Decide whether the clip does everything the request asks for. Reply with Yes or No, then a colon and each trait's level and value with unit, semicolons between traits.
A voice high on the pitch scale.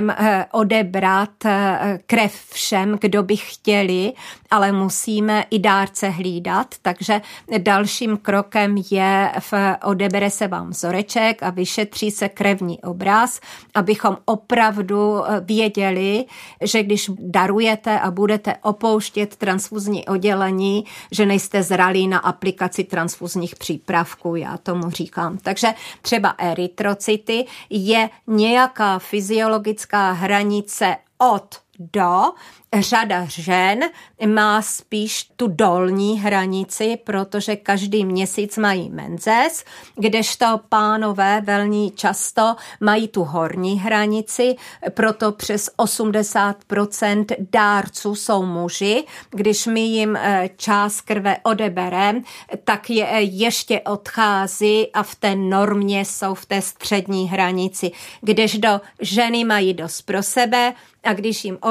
Yes: high, 205 Hz